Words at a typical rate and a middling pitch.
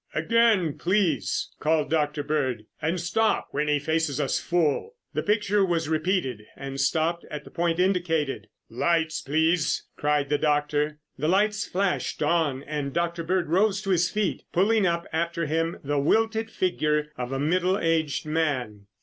Yes: average, 160 wpm; medium, 160 Hz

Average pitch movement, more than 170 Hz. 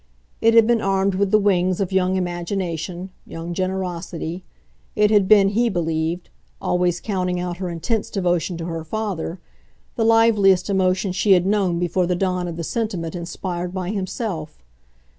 No: narrow, 2.3 semitones; medium, 185 Hz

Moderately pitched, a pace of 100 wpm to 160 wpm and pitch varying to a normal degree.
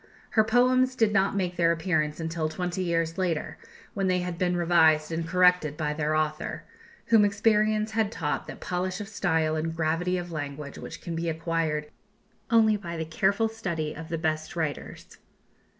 No: medium, 170 Hz; average, 175 wpm; average, 3.8 semitones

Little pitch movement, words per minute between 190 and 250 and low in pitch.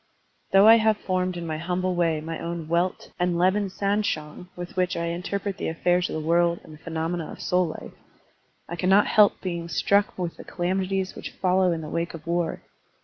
No: narrow, 2.0 semitones; average, 200 wpm; medium, 175 Hz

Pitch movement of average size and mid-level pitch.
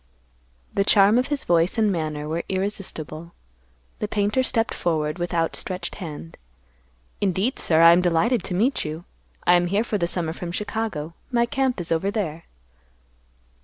Yes: average, 4.3 semitones; medium, 180 Hz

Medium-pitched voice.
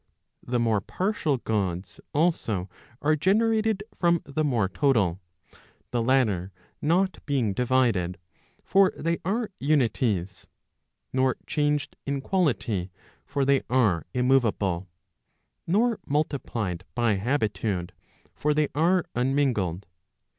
No: low, 130 Hz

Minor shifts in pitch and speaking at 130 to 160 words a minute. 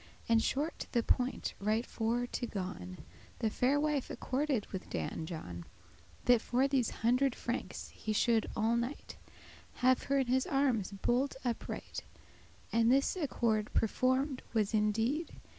No: average, 3.4 semitones; average, 150 wpm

